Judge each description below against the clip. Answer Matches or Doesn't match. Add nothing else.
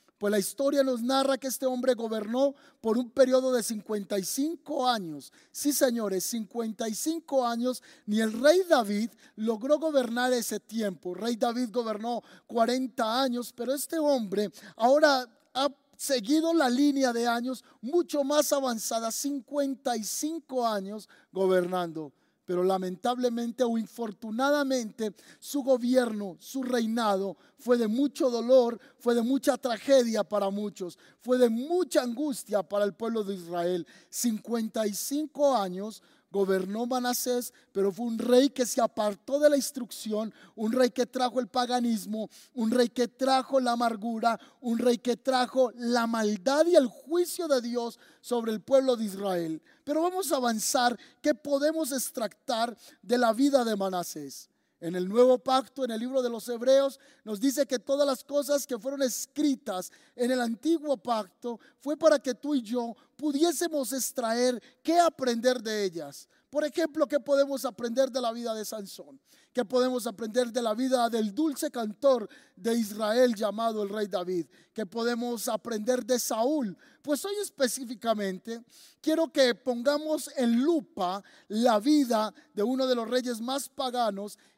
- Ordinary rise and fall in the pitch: Matches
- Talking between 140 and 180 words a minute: Matches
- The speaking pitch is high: Matches